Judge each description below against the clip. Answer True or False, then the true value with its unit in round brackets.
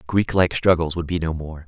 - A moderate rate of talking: False (215 wpm)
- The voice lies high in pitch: False (85 Hz)